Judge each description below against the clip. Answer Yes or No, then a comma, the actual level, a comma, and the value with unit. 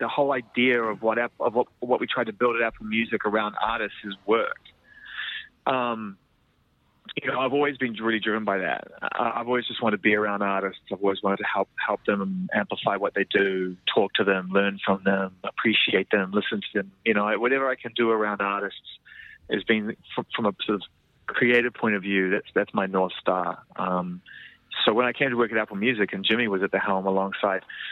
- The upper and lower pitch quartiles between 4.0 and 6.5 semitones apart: No, average, 3.4 semitones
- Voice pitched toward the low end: Yes, low, 110 Hz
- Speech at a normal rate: No, fast, 210 wpm